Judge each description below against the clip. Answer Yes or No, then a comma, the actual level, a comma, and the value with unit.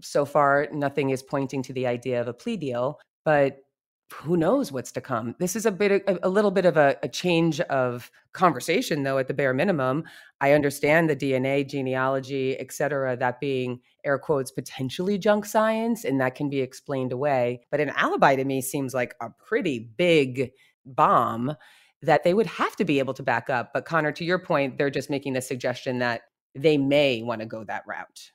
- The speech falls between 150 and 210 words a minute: Yes, average, 200 wpm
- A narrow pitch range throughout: No, average, 3.7 semitones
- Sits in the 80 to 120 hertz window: No, medium, 140 Hz